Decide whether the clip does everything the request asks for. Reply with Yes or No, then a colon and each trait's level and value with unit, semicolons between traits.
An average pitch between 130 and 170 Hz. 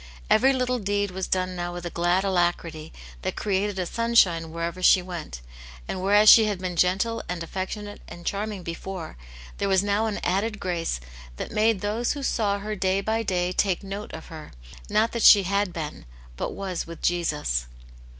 No: high, 190 Hz